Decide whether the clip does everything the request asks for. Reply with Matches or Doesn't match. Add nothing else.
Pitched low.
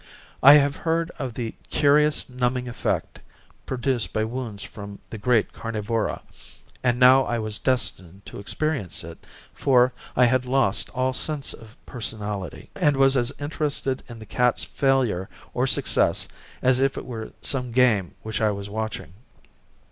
Matches